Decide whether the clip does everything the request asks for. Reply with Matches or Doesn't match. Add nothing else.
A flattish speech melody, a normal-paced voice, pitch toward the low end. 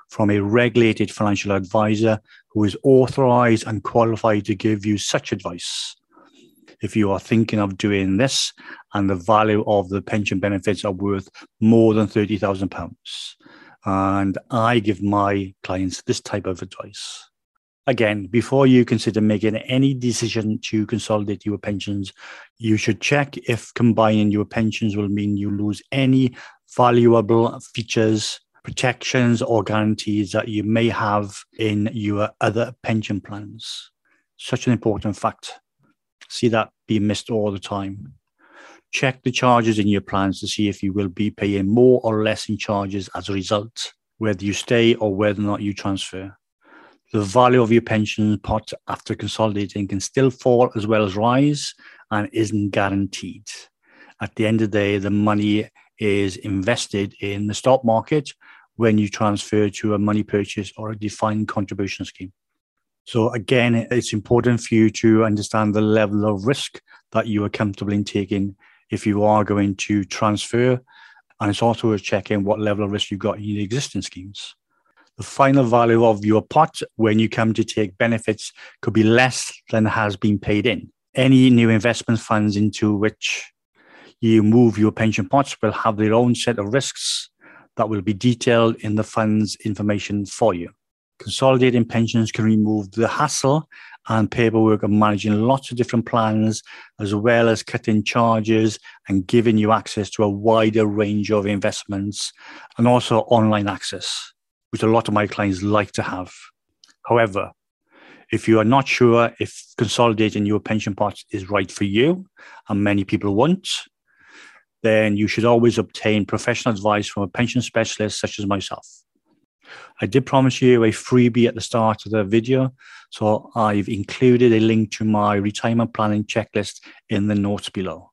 Matches